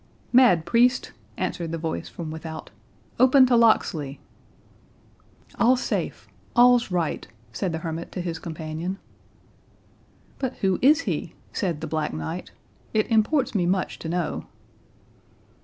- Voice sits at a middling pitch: Yes, medium, 180 Hz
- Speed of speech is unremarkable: No, slow, 125 wpm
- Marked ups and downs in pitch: Yes, wide, 6.9 semitones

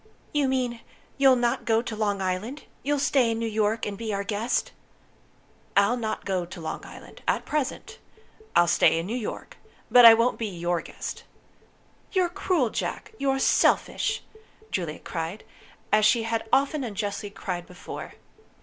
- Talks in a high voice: Yes, high, 225 Hz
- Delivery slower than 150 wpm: No, average, 160 wpm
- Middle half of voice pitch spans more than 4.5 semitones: No, average, 3.9 semitones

